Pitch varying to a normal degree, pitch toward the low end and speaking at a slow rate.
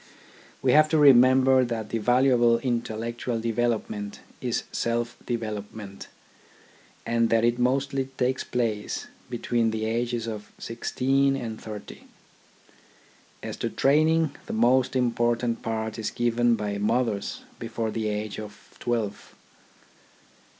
No: narrow, 2.3 semitones; low, 120 Hz; slow, 120 wpm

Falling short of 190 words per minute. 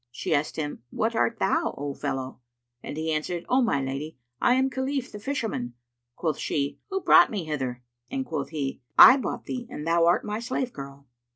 No: average, 195 wpm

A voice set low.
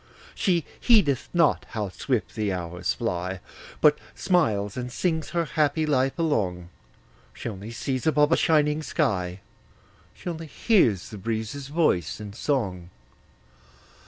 Yes: low, 130 Hz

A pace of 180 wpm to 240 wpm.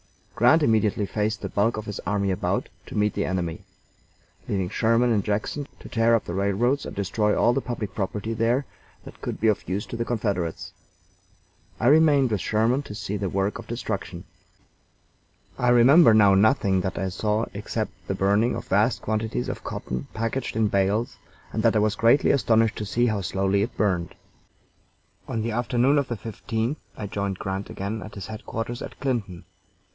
Yes: average, 185 wpm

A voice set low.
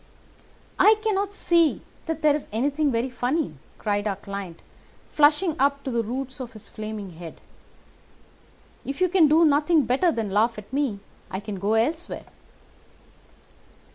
No: very high, 265 Hz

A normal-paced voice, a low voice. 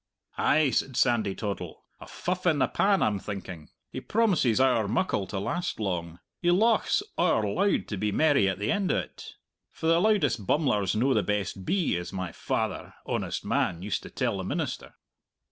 Yes: average, 180 wpm; low, 120 Hz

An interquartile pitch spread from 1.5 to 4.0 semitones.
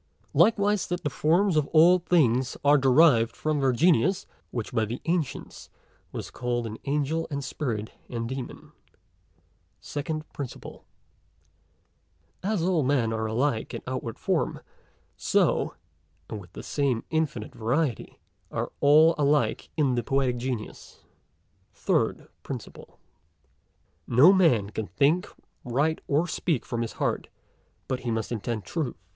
No: average, 5.1 semitones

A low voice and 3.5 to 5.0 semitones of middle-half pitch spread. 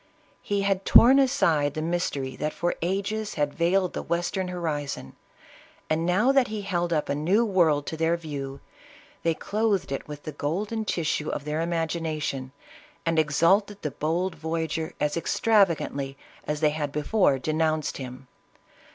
No: medium, 165 Hz; average, 4.2 semitones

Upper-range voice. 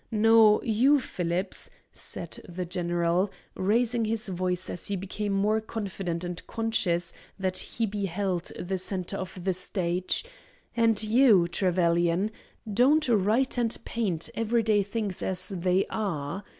Yes: high, 195 Hz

